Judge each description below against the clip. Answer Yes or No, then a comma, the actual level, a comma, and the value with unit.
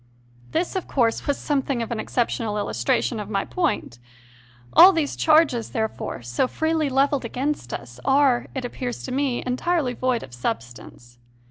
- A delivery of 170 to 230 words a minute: No, average, 160 wpm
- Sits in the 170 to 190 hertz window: No, very high, 250 Hz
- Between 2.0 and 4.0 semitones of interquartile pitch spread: No, average, 5.2 semitones